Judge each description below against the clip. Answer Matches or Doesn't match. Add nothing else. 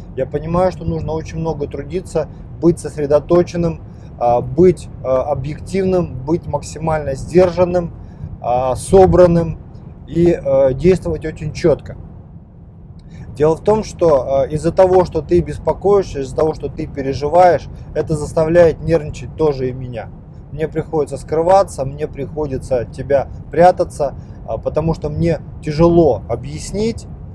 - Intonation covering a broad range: Doesn't match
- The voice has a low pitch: Doesn't match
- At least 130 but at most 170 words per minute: Doesn't match